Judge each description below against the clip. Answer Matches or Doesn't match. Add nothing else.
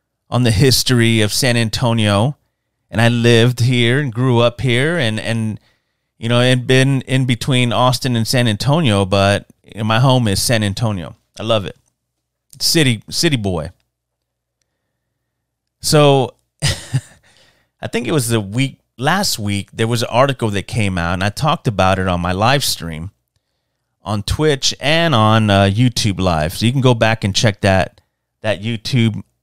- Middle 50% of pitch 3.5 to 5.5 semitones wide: Matches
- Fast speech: Doesn't match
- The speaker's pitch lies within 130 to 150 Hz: Doesn't match